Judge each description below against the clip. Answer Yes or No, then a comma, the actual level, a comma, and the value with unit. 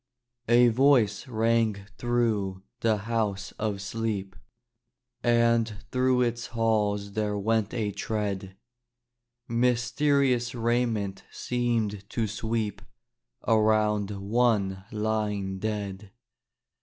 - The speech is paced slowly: Yes, slow, 90 wpm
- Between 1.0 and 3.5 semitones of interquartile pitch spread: Yes, narrow, 2.5 semitones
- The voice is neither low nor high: No, low, 110 Hz